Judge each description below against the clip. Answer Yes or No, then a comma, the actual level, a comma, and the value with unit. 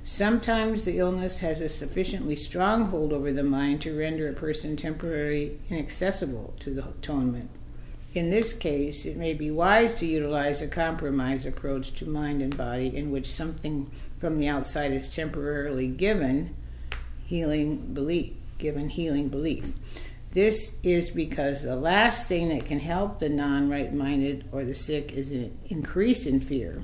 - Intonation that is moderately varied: Yes, average, 3.1 semitones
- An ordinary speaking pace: Yes, average, 155 wpm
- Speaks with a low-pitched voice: No, medium, 150 Hz